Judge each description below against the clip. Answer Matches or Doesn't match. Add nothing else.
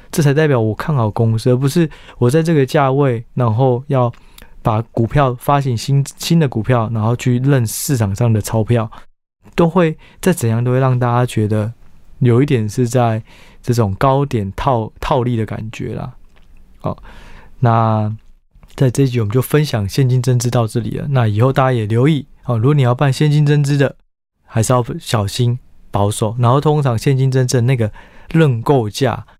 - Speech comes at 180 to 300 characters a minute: Matches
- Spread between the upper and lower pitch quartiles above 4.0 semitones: Doesn't match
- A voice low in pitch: Matches